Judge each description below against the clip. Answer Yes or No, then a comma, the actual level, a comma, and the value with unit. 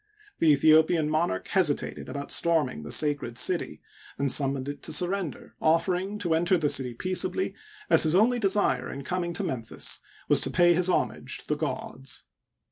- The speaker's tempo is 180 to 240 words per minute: No, average, 170 wpm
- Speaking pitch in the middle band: Yes, medium, 160 Hz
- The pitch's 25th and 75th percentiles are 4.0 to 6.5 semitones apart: Yes, average, 4.4 semitones